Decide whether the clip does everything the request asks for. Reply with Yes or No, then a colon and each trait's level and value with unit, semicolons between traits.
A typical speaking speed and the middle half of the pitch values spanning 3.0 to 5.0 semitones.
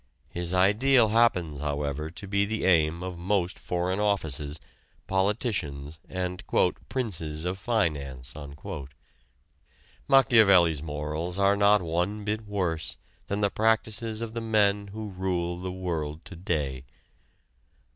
No: slow, 120 wpm; average, 4.4 semitones